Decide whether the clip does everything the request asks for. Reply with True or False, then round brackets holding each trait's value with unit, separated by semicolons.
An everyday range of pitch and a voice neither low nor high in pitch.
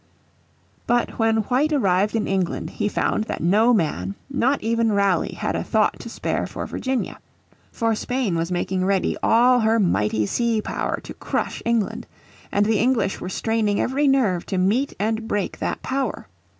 False (3.9 semitones; 220 Hz)